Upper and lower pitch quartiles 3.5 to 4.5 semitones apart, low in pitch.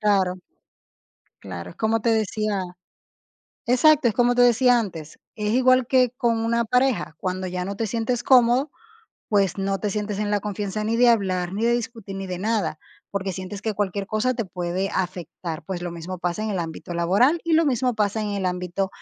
No: average, 4.0 semitones; high, 210 Hz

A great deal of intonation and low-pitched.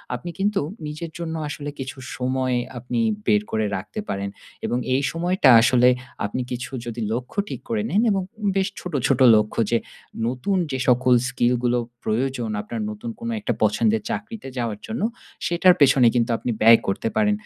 Yes: wide, 6.6 semitones; low, 130 Hz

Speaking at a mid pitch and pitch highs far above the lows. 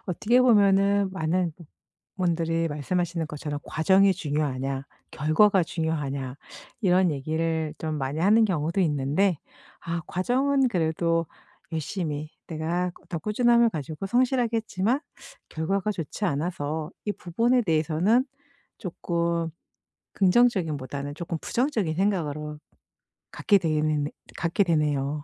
No: medium, 170 Hz; average, 4.4 semitones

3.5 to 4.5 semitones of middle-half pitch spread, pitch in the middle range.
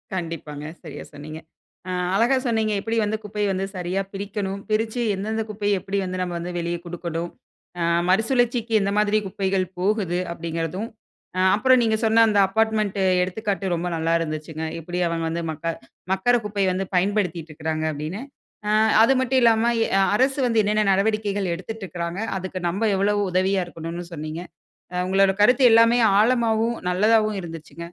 No: average, 4.2 semitones; high, 195 Hz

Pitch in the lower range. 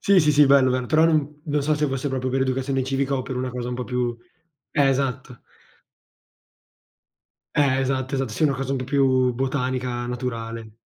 Yes: low, 130 Hz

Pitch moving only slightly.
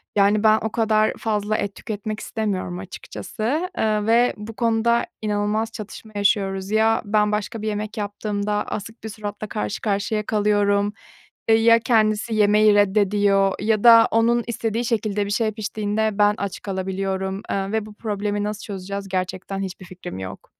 Yes: narrow, 1.5 semitones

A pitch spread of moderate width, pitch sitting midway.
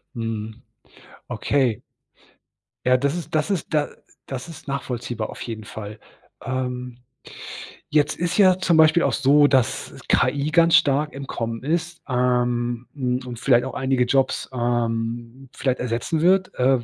No: average, 3.8 semitones; low, 130 Hz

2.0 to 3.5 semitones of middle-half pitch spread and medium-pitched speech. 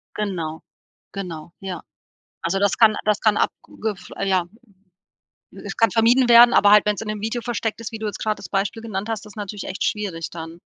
No: average, 2.7 semitones; high, 210 Hz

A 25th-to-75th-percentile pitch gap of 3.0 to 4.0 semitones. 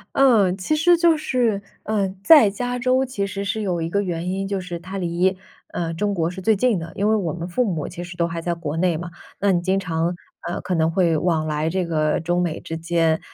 Yes: average, 3.3 semitones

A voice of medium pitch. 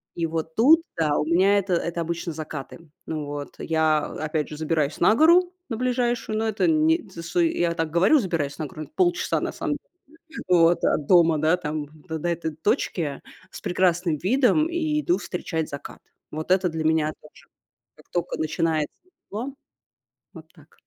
Yes: medium, 170 Hz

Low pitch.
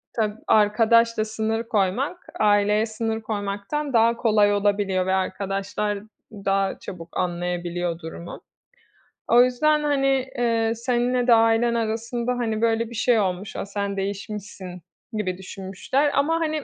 No: high, 215 Hz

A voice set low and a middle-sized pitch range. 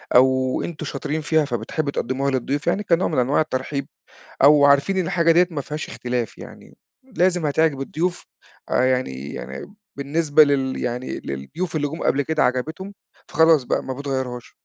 No: medium, 145 Hz; average, 3.7 semitones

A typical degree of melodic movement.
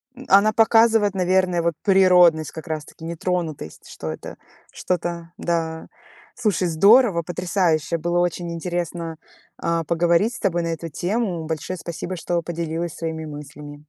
No: narrow, 2.2 semitones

